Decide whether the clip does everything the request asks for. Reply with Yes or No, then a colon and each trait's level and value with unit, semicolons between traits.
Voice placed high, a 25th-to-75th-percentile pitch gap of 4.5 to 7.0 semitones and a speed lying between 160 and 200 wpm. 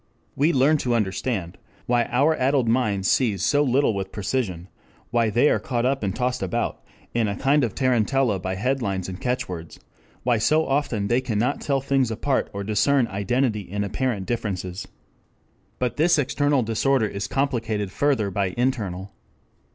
No: low, 120 Hz; average, 5.1 semitones; average, 165 wpm